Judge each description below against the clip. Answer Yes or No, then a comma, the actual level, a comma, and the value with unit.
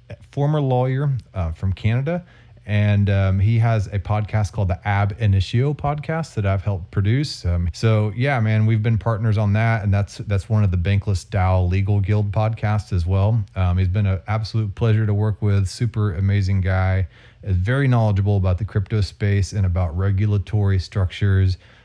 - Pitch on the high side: No, low, 105 Hz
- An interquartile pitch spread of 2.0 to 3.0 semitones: Yes, narrow, 2.6 semitones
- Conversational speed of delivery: Yes, average, 180 wpm